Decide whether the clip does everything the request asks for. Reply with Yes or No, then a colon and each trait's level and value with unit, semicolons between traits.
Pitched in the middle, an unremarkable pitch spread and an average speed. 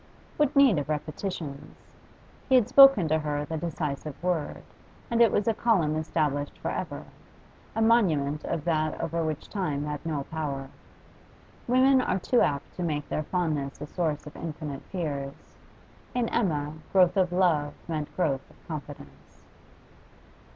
Yes: medium, 155 Hz; average, 4.0 semitones; average, 150 wpm